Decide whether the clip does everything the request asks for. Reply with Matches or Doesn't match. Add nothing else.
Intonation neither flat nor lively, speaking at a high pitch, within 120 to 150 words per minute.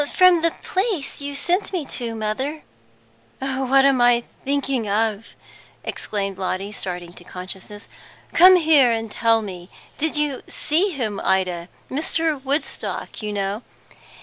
Doesn't match